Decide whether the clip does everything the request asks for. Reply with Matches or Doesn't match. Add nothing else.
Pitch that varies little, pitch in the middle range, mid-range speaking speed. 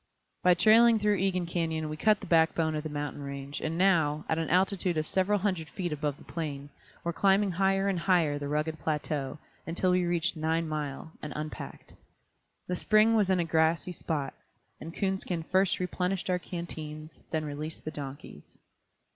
Doesn't match